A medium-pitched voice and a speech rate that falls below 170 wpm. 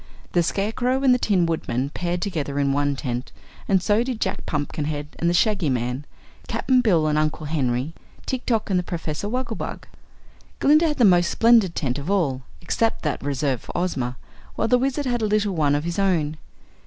No: medium, 175 Hz; average, 190 wpm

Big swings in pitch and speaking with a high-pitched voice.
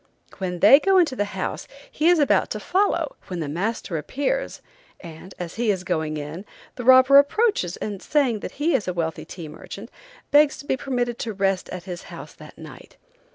Yes: wide, 8.0 semitones; high, 210 Hz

